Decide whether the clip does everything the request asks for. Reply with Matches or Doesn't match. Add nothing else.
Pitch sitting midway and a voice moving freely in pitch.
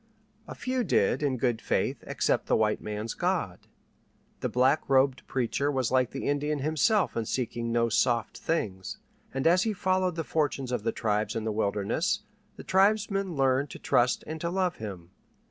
Doesn't match